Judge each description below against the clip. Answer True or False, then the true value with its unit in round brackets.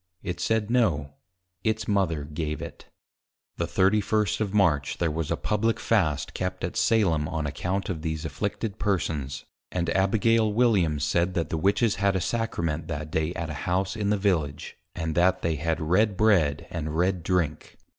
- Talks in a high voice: False (90 Hz)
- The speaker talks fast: False (175 wpm)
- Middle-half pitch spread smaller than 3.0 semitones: False (4.7 semitones)